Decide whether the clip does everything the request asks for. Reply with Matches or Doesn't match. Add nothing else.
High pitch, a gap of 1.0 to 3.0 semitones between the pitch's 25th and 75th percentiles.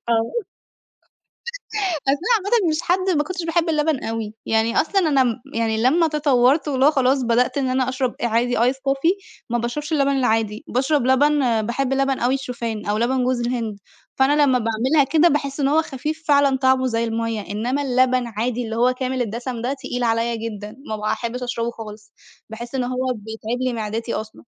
Doesn't match